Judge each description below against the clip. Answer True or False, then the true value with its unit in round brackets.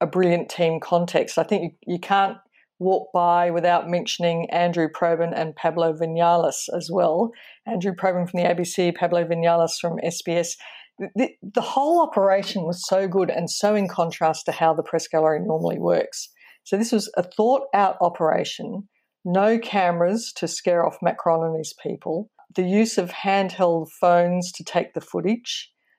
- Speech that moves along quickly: False (170 wpm)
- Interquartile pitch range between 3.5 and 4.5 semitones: False (2.7 semitones)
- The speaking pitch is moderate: True (175 Hz)